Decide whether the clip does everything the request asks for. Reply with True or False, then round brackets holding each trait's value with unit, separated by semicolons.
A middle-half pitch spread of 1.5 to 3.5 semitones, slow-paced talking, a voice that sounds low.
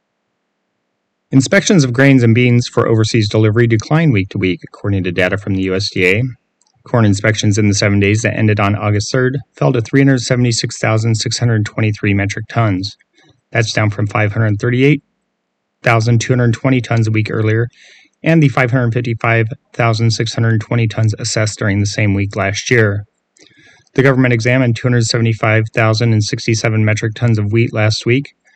True (2.5 semitones; 130 wpm; 115 Hz)